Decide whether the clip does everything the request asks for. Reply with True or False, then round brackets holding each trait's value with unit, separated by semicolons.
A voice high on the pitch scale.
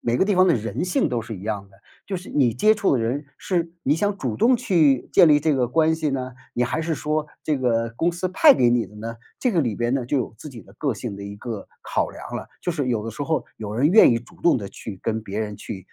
False (130 Hz)